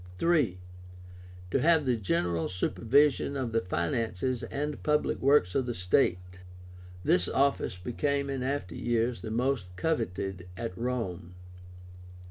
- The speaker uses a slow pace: Yes, slow, 125 wpm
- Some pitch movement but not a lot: No, wide, 7.2 semitones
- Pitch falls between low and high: No, low, 120 Hz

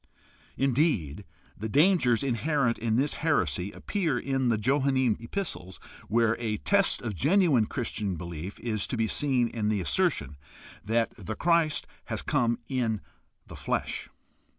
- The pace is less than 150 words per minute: Yes, average, 140 wpm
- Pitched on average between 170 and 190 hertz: No, low, 120 Hz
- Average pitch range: Yes, average, 4.6 semitones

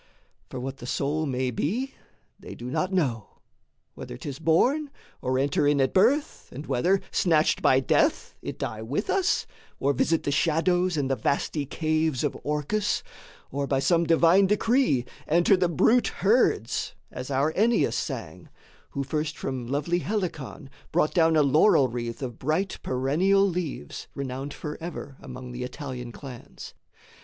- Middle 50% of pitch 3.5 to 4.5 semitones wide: No, average, 5.2 semitones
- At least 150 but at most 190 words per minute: Yes, average, 155 wpm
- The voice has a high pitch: No, medium, 150 Hz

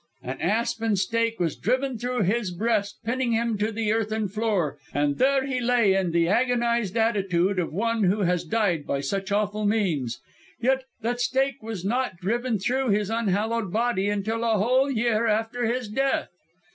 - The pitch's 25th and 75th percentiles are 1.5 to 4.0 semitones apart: Yes, average, 3.4 semitones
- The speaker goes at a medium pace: Yes, average, 170 wpm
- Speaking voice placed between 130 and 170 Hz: No, high, 220 Hz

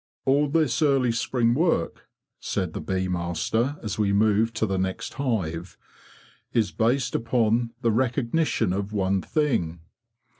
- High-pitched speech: No, low, 115 Hz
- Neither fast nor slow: Yes, average, 150 wpm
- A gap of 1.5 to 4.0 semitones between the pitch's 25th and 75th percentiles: No, average, 5.0 semitones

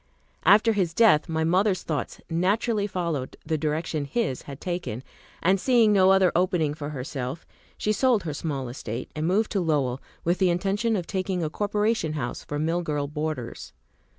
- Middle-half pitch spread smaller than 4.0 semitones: No, average, 4.7 semitones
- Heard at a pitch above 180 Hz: No, medium, 170 Hz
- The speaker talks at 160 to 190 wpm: Yes, average, 175 wpm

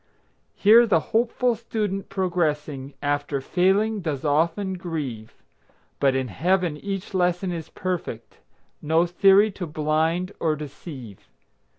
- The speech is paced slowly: Yes, slow, 115 wpm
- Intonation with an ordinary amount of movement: Yes, average, 4.5 semitones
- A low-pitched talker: No, medium, 170 Hz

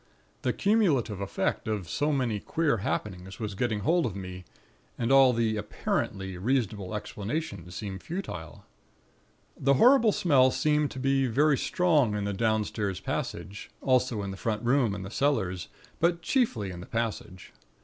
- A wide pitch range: Yes, wide, 6.0 semitones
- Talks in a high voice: No, low, 115 Hz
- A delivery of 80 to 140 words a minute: No, average, 155 wpm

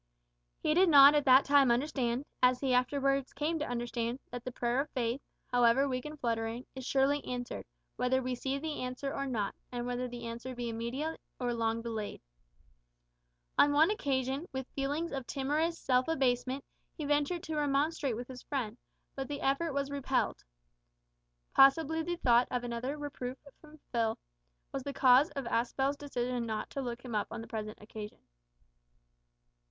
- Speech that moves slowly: No, average, 170 wpm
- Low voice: No, very high, 260 Hz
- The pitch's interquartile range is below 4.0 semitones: Yes, average, 2.8 semitones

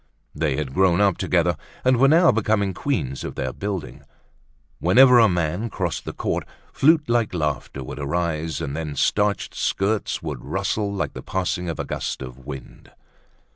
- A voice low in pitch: Yes, very low, 90 Hz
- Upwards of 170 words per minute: No, average, 165 wpm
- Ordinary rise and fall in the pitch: No, wide, 5.8 semitones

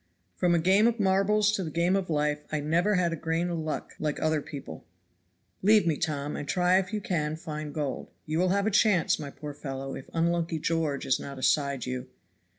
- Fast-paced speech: Yes, fast, 215 wpm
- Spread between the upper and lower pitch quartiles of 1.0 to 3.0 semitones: No, average, 3.9 semitones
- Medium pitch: Yes, medium, 165 Hz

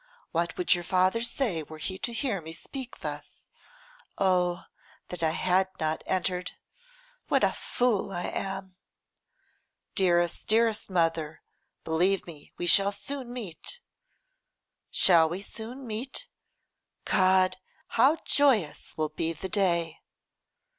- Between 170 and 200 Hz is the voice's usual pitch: Yes, medium, 185 Hz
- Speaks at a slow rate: Yes, slow, 125 wpm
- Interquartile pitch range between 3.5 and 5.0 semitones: Yes, average, 4.4 semitones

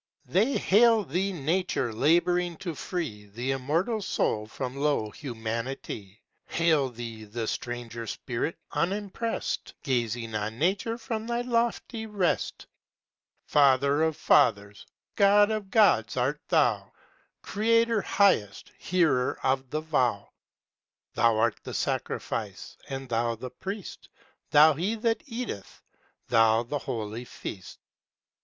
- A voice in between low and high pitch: Yes, medium, 145 Hz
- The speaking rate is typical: No, slow, 120 wpm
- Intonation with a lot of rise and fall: Yes, wide, 8.9 semitones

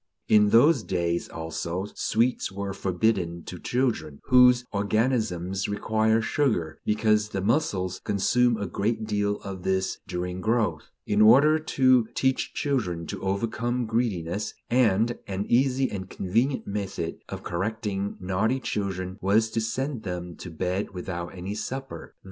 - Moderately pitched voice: No, low, 105 Hz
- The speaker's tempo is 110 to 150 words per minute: Yes, slow, 135 wpm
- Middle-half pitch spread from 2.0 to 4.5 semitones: Yes, average, 4.1 semitones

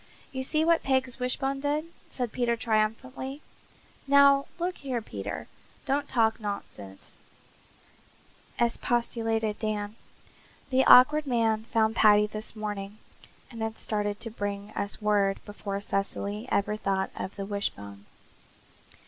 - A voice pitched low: No, high, 220 Hz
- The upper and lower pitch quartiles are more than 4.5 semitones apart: No, average, 3.9 semitones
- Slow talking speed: Yes, slow, 125 wpm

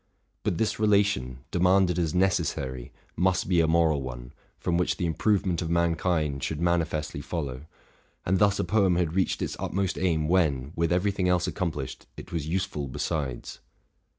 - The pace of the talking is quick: No, average, 165 wpm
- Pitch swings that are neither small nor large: Yes, average, 3.4 semitones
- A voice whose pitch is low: Yes, very low, 85 Hz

